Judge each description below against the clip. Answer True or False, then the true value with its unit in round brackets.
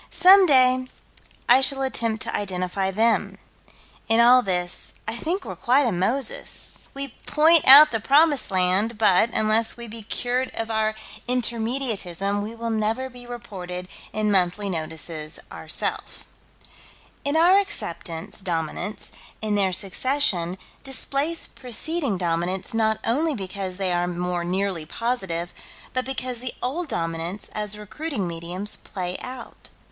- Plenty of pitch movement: True (5.8 semitones)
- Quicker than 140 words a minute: False (135 wpm)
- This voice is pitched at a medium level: False (220 Hz)